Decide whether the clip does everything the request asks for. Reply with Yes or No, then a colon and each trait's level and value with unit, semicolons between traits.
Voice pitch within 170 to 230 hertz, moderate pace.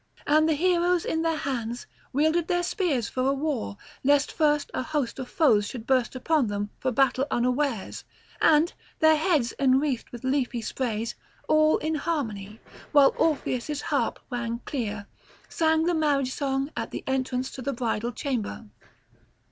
No: very high, 270 Hz; average, 155 wpm